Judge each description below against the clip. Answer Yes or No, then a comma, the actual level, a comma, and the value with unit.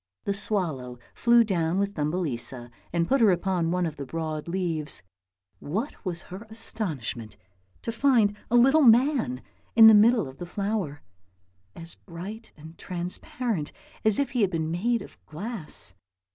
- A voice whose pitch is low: No, medium, 185 Hz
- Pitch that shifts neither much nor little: No, wide, 5.8 semitones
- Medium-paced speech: Yes, average, 155 wpm